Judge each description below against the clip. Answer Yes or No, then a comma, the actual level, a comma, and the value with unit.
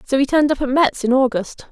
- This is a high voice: Yes, very high, 265 Hz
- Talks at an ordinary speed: No, fast, 280 wpm